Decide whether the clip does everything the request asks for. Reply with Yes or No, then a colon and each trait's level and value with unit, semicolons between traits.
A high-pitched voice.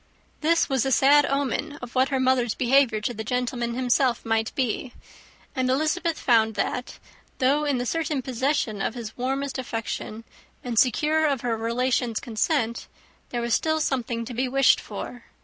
Yes: very high, 255 Hz